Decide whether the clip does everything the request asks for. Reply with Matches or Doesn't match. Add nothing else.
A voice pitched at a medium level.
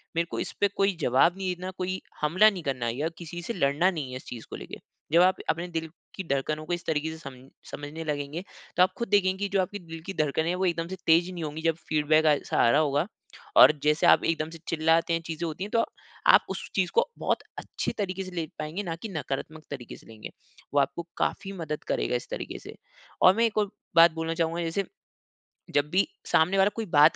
Matches